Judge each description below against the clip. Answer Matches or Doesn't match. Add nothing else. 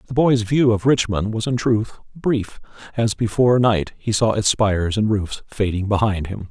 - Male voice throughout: Matches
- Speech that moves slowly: Doesn't match